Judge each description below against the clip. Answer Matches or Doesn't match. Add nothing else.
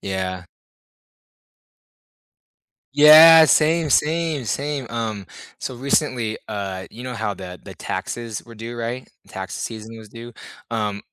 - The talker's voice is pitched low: Matches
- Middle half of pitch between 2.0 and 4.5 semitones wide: Doesn't match